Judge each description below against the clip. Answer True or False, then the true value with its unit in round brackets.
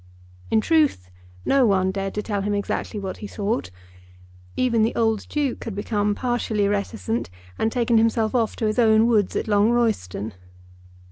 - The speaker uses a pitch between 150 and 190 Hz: False (220 Hz)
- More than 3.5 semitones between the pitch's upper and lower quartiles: False (2.4 semitones)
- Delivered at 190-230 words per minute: False (165 wpm)